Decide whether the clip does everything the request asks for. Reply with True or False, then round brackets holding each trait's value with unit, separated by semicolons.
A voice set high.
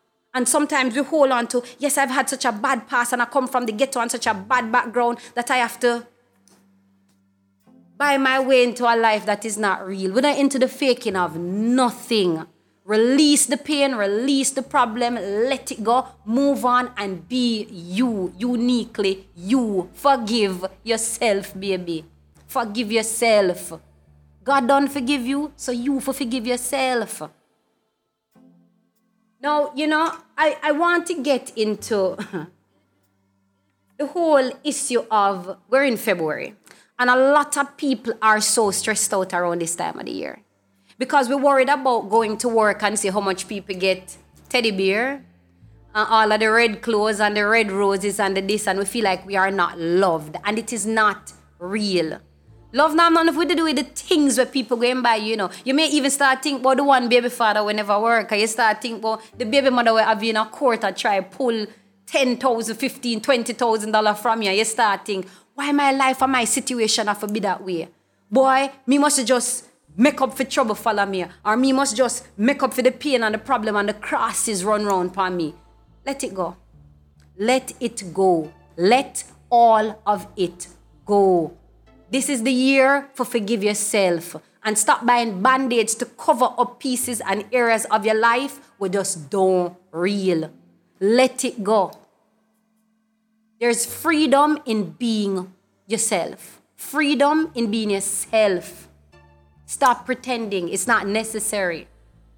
True (225 Hz)